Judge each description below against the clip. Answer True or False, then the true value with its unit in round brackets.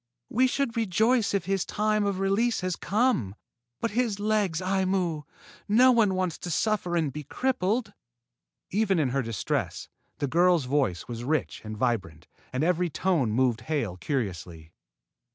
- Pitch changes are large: True (8.2 semitones)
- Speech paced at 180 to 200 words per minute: False (150 wpm)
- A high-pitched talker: False (180 Hz)